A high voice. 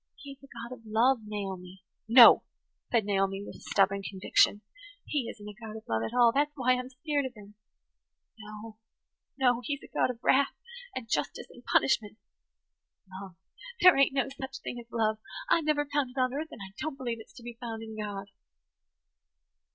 Yes: high, 235 Hz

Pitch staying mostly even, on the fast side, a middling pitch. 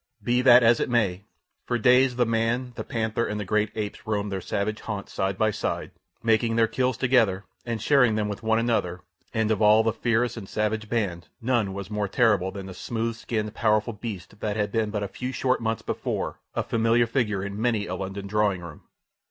No: narrow, 2.3 semitones; fast, 210 wpm; low, 110 Hz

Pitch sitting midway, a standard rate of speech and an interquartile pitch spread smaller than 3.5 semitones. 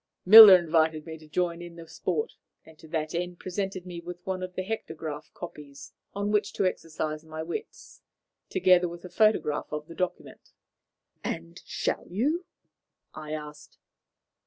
Yes: medium, 175 Hz; average, 160 wpm; average, 3.0 semitones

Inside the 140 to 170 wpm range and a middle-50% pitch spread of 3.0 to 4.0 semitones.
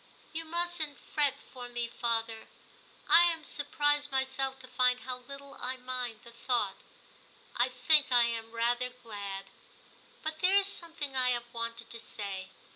Yes: average, 155 wpm; average, 3.7 semitones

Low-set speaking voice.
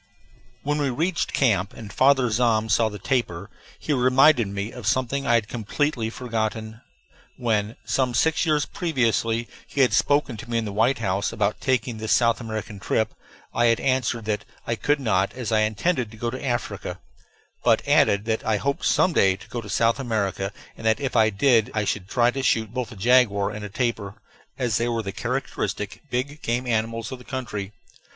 Yes: low, 115 Hz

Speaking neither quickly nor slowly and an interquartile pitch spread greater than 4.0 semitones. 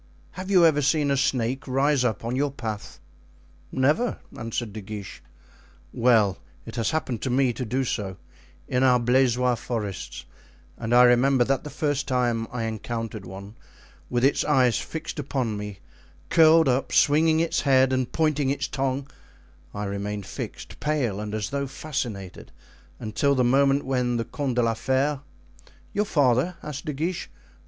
No: average, 165 wpm; average, 3.7 semitones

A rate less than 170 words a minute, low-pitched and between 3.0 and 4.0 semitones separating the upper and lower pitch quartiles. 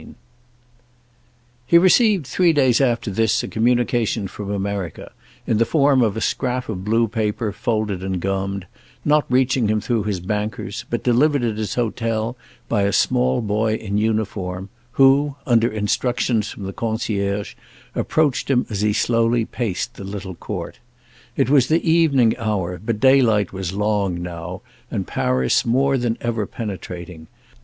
Yes: average, 155 wpm; low, 110 Hz; average, 3.6 semitones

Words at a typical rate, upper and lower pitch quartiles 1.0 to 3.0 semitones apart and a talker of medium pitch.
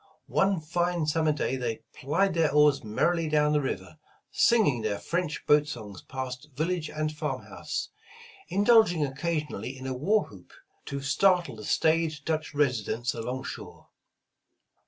No: average, 150 wpm; average, 4.4 semitones; medium, 150 Hz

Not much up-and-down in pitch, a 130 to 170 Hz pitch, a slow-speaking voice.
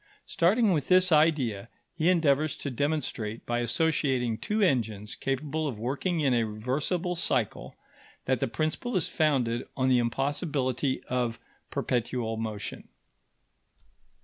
No: average, 5.0 semitones; low, 135 Hz; slow, 125 wpm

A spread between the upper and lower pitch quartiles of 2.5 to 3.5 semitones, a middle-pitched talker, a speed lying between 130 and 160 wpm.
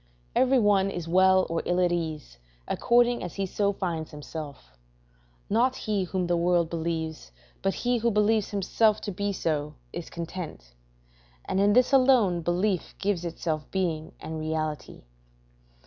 No: average, 4.2 semitones; medium, 180 Hz; average, 150 wpm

